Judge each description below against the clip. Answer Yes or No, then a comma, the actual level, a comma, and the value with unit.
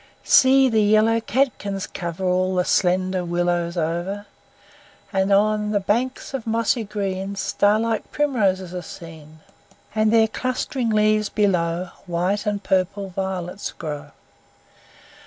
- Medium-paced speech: No, slow, 125 wpm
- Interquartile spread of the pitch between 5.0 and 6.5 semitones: No, average, 3.2 semitones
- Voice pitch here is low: No, high, 200 Hz